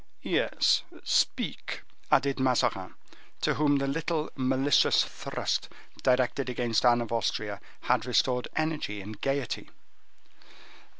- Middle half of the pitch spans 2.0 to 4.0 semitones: Yes, average, 2.8 semitones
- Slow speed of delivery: Yes, slow, 110 wpm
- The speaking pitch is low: Yes, low, 130 Hz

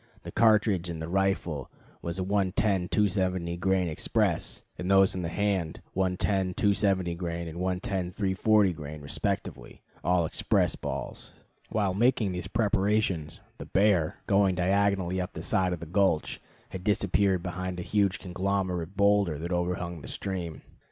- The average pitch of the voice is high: No, very low, 95 Hz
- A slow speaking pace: No, average, 150 wpm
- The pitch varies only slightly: Yes, narrow, 2.3 semitones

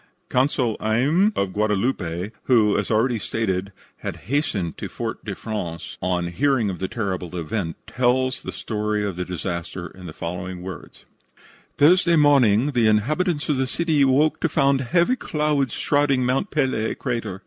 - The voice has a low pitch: Yes, low, 115 Hz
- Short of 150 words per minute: No, average, 160 wpm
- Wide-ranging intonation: Yes, wide, 6.7 semitones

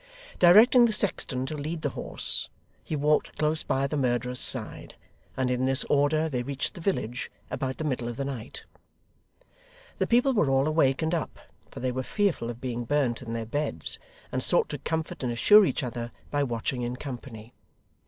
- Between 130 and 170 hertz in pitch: Yes, low, 135 Hz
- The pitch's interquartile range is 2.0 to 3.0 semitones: No, average, 4.2 semitones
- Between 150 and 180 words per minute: No, average, 190 wpm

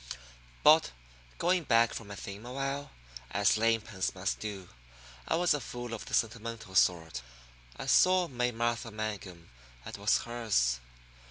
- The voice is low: Yes, low, 115 Hz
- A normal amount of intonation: Yes, average, 3.6 semitones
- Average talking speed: Yes, average, 155 wpm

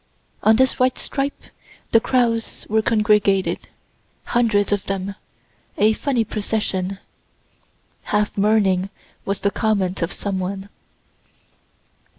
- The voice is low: No, high, 210 Hz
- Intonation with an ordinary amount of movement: No, narrow, 2.3 semitones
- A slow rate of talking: Yes, slow, 110 wpm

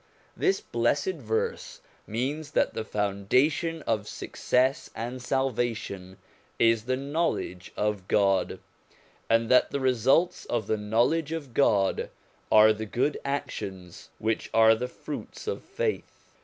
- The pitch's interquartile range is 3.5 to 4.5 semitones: No, average, 5.1 semitones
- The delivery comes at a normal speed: No, slow, 130 wpm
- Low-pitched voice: Yes, low, 120 Hz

